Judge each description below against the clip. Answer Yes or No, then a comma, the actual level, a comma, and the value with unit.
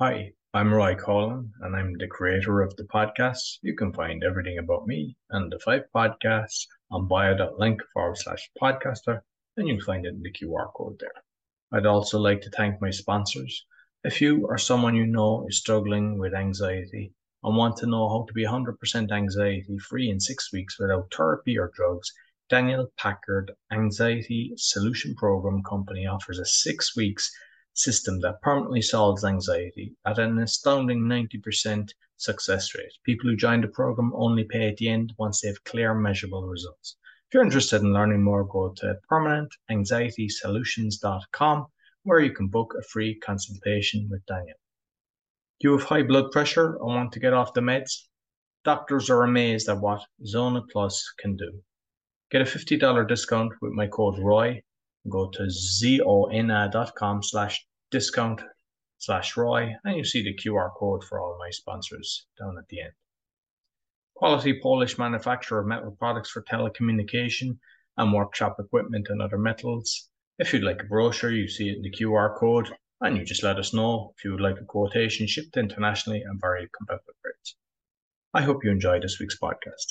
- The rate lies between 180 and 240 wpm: No, average, 170 wpm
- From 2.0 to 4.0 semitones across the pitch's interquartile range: Yes, average, 2.9 semitones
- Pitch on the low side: Yes, low, 110 Hz